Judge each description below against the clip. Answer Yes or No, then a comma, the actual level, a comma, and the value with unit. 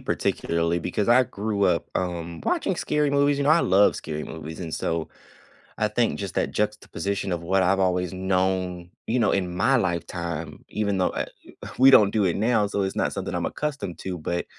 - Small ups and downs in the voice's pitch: No, average, 3.6 semitones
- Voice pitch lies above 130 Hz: No, very low, 95 Hz